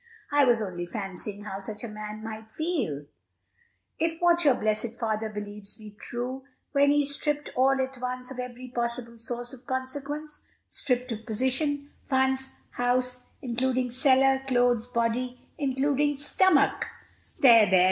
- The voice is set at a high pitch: Yes, very high, 250 Hz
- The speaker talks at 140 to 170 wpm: Yes, average, 145 wpm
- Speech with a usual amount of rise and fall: Yes, average, 3.3 semitones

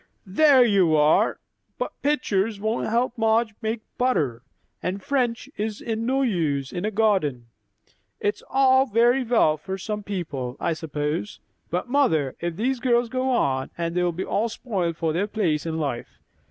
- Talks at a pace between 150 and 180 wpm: Yes, average, 155 wpm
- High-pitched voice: Yes, high, 205 Hz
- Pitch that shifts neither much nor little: No, wide, 6.7 semitones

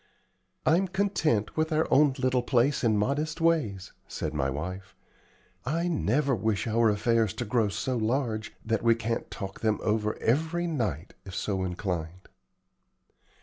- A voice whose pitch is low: Yes, low, 115 Hz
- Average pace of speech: Yes, average, 145 wpm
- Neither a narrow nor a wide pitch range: No, wide, 5.9 semitones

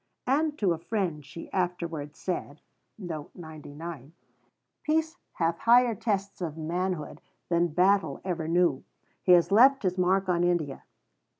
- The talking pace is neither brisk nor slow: No, slow, 125 wpm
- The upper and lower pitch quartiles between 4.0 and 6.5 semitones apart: No, average, 3.2 semitones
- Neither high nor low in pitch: Yes, medium, 180 Hz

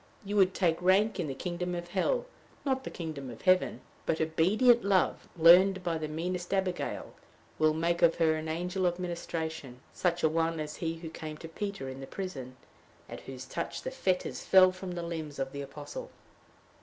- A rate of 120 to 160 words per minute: No, average, 195 wpm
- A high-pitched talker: No, medium, 170 Hz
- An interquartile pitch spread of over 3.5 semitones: No, average, 2.8 semitones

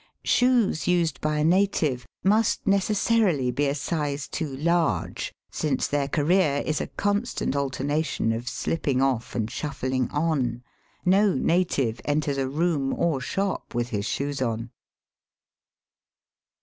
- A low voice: No, medium, 145 Hz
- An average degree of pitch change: Yes, average, 4.9 semitones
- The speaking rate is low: Yes, slow, 130 wpm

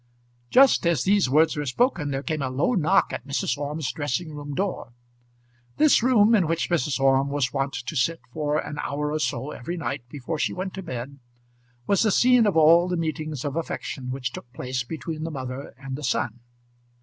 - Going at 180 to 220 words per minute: Yes, average, 200 wpm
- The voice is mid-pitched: Yes, medium, 150 Hz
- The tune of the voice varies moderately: Yes, average, 4.1 semitones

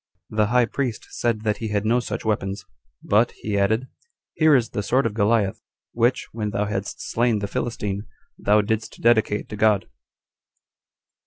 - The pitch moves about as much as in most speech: No, narrow, 2.2 semitones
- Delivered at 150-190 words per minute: Yes, average, 165 wpm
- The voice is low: Yes, low, 110 Hz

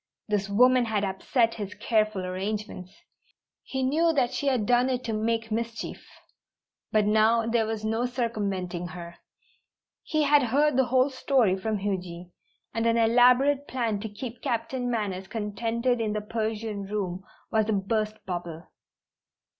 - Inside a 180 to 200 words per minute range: No, average, 150 wpm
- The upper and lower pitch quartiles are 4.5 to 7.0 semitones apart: No, average, 3.3 semitones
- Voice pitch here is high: Yes, high, 220 Hz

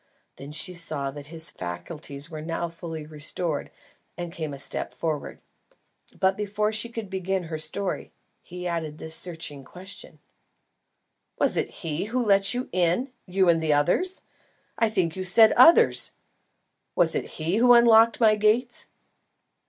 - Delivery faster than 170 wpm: No, average, 150 wpm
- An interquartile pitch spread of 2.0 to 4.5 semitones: No, average, 5.0 semitones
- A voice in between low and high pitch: Yes, medium, 175 Hz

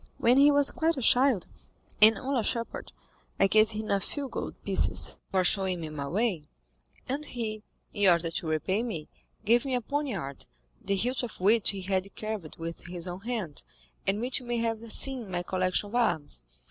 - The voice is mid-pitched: No, high, 215 Hz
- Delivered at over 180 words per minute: Yes, average, 200 wpm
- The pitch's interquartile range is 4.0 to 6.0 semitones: Yes, average, 4.9 semitones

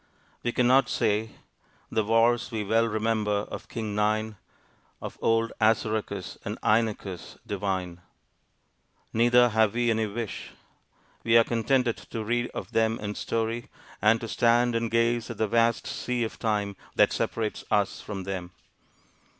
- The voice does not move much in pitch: Yes, narrow, 1.8 semitones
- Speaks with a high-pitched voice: No, low, 110 Hz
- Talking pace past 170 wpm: No, average, 145 wpm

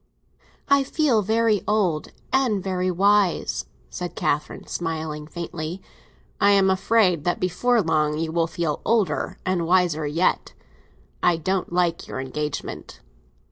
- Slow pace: Yes, slow, 125 wpm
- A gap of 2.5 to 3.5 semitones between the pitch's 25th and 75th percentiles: No, average, 4.1 semitones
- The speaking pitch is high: No, medium, 180 Hz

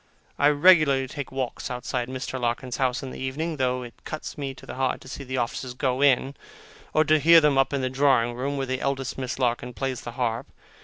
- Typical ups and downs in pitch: No, narrow, 1.8 semitones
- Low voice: Yes, low, 130 Hz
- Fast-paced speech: Yes, fast, 225 wpm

